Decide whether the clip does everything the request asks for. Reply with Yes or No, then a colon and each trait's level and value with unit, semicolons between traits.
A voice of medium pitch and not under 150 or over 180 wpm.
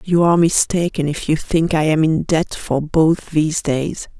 No: medium, 160 Hz; average, 200 wpm